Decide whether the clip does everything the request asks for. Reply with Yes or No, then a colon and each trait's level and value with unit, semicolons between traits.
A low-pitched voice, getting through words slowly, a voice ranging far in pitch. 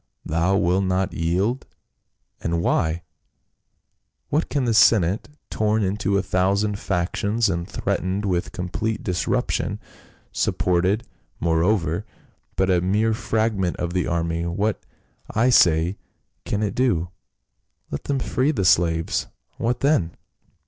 No: very low, 95 Hz; slow, 125 wpm; average, 3.8 semitones